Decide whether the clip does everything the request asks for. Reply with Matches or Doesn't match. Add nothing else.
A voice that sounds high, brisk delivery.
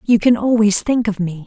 Matches